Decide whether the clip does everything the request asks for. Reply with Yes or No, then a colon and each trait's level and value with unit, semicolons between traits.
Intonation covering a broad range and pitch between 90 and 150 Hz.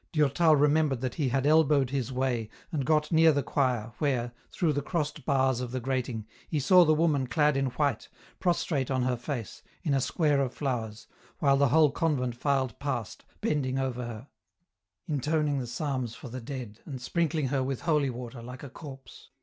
No: average, 3.0 semitones; low, 135 Hz